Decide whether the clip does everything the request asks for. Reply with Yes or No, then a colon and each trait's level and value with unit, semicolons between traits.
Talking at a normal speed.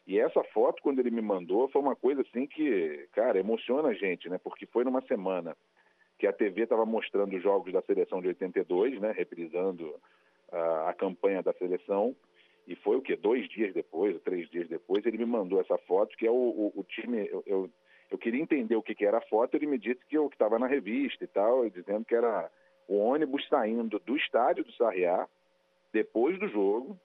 No: fast, 215 wpm